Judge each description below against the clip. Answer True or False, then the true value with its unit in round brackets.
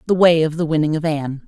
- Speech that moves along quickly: True (285 wpm)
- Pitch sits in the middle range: True (160 Hz)